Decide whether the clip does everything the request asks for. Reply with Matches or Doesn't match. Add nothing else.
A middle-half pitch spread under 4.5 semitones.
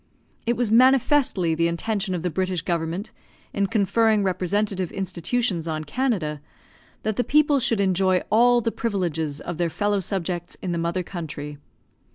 Doesn't match